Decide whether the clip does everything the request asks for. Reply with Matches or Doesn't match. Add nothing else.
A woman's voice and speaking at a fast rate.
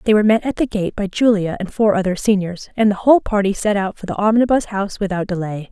Matches